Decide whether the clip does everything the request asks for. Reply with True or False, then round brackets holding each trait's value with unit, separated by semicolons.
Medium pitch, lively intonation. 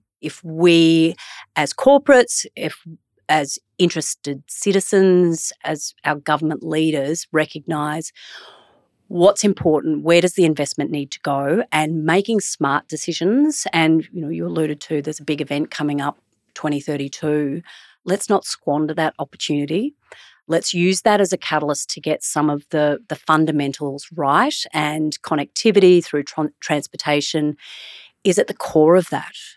False (155 Hz; 3.0 semitones)